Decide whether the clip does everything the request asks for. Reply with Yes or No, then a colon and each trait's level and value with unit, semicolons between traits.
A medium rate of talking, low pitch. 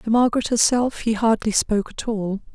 No: average, 190 wpm; high, 220 Hz